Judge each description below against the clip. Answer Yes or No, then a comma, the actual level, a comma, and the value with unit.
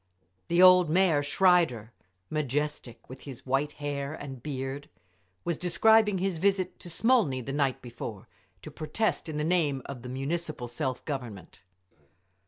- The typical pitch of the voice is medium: Yes, medium, 150 Hz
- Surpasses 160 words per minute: No, average, 145 wpm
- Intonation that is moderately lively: Yes, average, 4.9 semitones